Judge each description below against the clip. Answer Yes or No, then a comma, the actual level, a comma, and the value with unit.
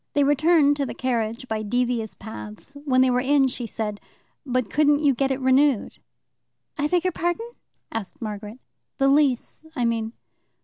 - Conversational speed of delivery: Yes, average, 170 wpm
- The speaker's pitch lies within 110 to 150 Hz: No, very high, 255 Hz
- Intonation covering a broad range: No, average, 4.3 semitones